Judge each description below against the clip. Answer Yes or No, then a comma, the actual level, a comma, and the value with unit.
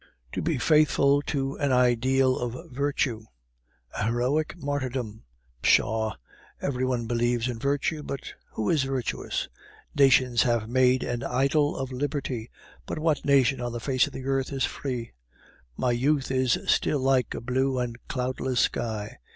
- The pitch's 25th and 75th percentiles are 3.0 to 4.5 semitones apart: No, narrow, 2.4 semitones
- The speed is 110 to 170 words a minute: Yes, average, 150 wpm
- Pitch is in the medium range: No, low, 130 Hz